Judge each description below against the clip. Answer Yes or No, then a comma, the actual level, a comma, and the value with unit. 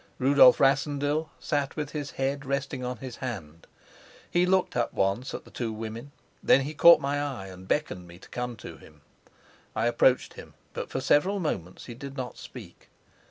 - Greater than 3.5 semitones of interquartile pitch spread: Yes, average, 3.9 semitones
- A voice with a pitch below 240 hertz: Yes, low, 135 Hz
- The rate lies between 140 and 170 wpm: No, average, 185 wpm